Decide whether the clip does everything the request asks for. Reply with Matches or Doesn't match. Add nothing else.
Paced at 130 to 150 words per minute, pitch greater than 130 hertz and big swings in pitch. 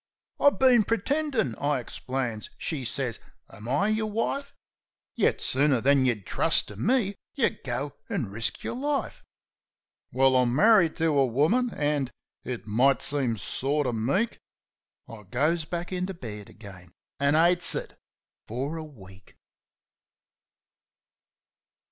Matches